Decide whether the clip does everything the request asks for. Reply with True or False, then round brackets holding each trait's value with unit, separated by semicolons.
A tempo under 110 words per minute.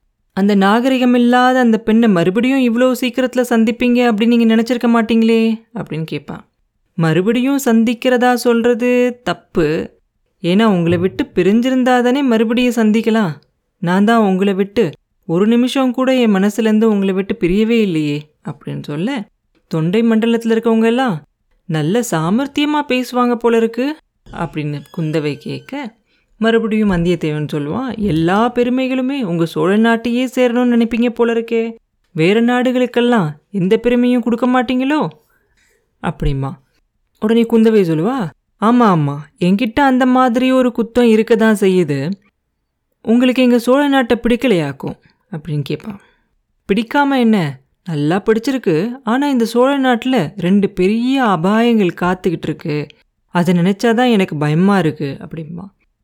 False (120 wpm)